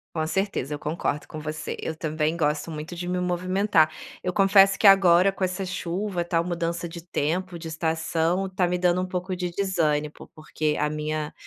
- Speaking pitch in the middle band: Yes, medium, 170 Hz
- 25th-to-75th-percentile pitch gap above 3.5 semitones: No, average, 2.8 semitones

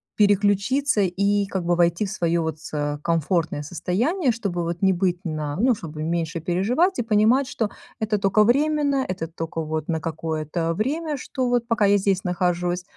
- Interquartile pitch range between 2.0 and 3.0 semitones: No, average, 5.0 semitones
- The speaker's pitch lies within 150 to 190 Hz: Yes, medium, 185 Hz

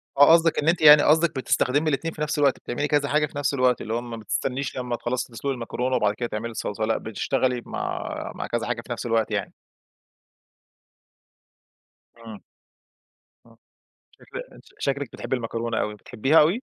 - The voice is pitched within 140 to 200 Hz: No, low, 125 Hz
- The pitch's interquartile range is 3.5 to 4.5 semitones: Yes, average, 3.9 semitones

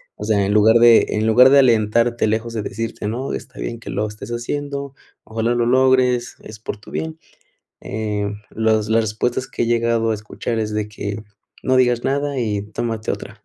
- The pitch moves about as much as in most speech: No, narrow, 2.3 semitones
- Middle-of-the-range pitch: No, low, 115 Hz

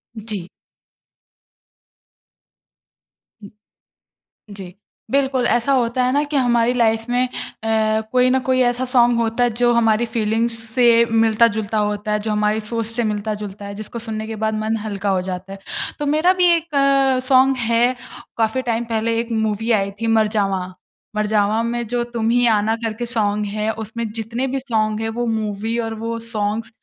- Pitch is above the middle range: Yes, high, 225 Hz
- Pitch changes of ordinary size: No, narrow, 2.3 semitones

